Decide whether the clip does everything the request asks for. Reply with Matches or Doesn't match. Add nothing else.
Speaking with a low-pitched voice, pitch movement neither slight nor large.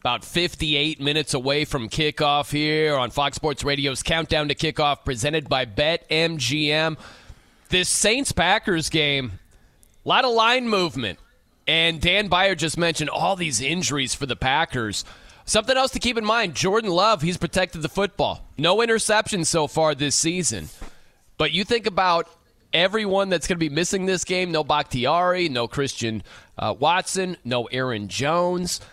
Doesn't match